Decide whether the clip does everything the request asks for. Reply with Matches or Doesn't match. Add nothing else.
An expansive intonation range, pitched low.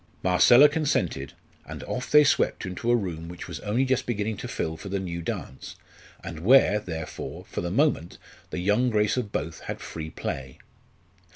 Matches